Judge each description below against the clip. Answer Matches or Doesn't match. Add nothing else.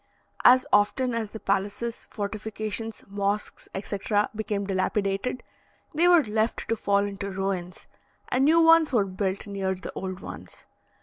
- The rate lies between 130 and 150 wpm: Matches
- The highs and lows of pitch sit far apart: Doesn't match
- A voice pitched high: Matches